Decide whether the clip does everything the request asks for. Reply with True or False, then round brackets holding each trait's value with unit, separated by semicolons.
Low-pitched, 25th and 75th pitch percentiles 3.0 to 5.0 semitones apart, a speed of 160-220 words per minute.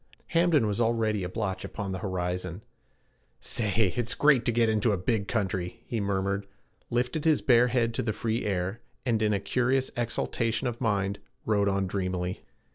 True (110 Hz; 3.4 semitones; 175 wpm)